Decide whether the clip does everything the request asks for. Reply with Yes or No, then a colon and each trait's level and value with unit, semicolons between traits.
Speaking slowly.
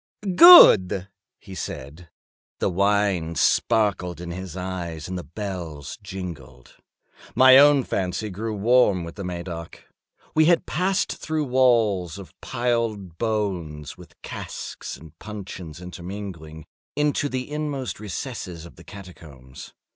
Yes: slow, 125 wpm